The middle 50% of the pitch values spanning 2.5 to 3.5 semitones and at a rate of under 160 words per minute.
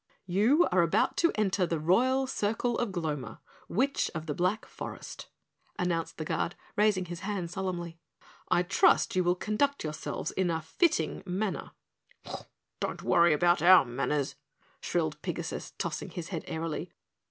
No: average, 4.0 semitones; average, 150 wpm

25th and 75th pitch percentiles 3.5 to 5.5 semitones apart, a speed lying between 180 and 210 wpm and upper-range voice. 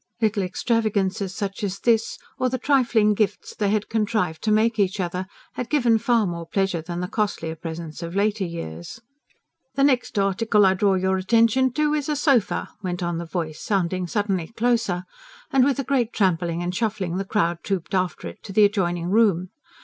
Yes: average, 4.1 semitones; average, 190 wpm; high, 200 Hz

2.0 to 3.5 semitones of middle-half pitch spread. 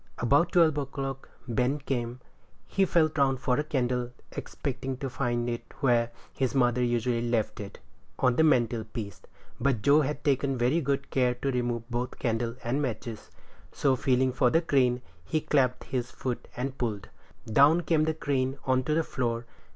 Yes: narrow, 2.6 semitones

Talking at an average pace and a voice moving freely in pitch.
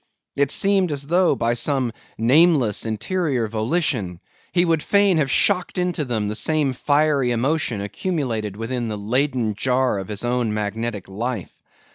Yes: average, 150 wpm; wide, 5.9 semitones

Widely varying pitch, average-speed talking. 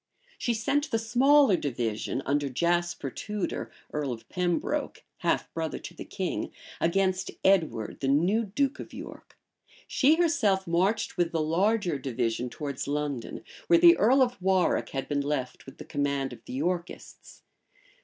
Yes: wide, 7.4 semitones; average, 155 wpm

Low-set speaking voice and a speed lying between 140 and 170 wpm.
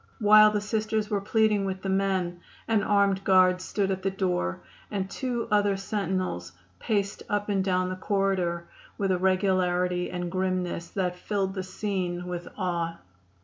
No: high, 190 Hz; average, 160 wpm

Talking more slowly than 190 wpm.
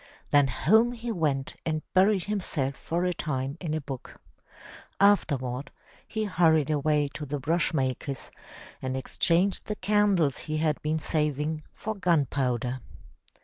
Yes: average, 145 wpm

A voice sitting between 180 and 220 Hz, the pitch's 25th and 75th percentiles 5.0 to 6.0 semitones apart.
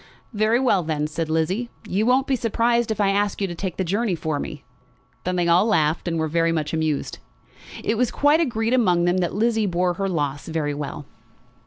Yes: medium, 185 Hz; wide, 5.6 semitones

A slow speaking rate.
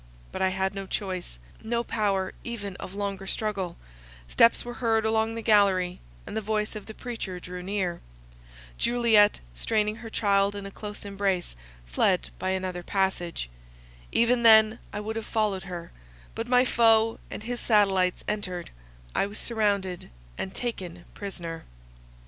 No: average, 155 wpm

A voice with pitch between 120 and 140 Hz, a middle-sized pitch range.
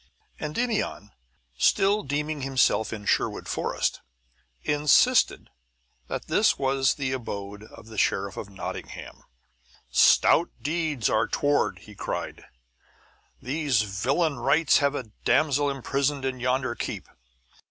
Yes: low, 135 Hz; average, 4.6 semitones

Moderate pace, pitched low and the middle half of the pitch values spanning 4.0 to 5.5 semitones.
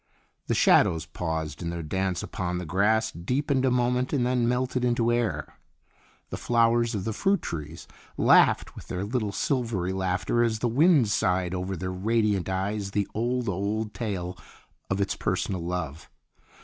Yes: average, 160 wpm; low, 105 Hz; average, 4.7 semitones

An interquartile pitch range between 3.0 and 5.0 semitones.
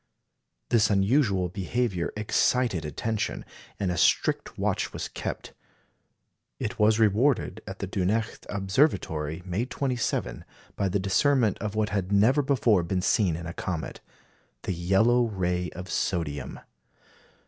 Yes: average, 4.0 semitones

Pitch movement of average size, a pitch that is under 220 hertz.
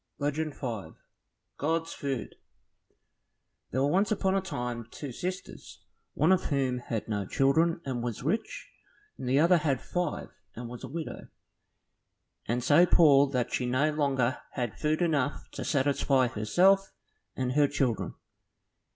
Yes: average, 4.7 semitones; medium, 140 Hz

